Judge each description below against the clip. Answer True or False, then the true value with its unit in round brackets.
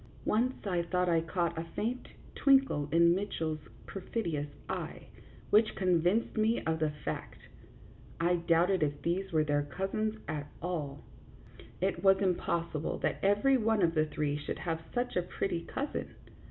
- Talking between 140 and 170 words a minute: True (155 wpm)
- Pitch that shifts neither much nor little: True (4.1 semitones)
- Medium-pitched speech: True (175 Hz)